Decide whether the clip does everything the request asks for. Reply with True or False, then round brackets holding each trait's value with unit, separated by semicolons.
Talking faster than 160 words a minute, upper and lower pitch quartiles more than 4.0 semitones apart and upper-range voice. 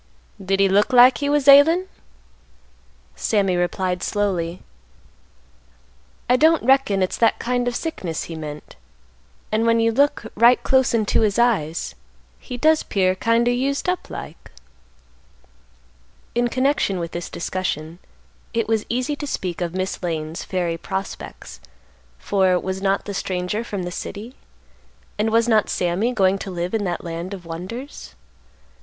False (150 wpm; 5.2 semitones; 205 Hz)